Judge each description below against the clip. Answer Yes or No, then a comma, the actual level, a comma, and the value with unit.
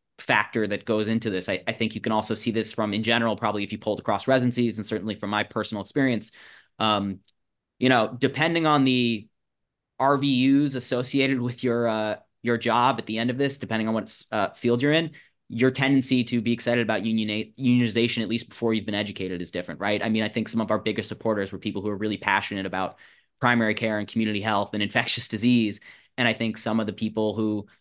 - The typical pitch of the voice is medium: No, low, 110 Hz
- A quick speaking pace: Yes, fast, 220 wpm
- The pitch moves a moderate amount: No, narrow, 2.3 semitones